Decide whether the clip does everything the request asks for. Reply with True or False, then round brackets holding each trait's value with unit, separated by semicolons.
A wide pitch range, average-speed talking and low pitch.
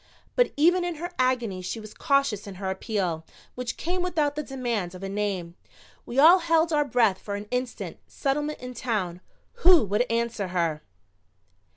False (7.1 semitones; 175 wpm; 240 Hz)